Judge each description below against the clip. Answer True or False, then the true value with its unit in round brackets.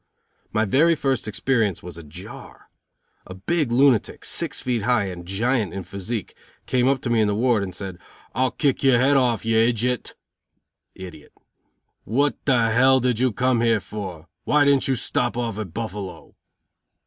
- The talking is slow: False (170 wpm)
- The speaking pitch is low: True (115 Hz)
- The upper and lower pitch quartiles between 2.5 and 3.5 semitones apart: False (4.5 semitones)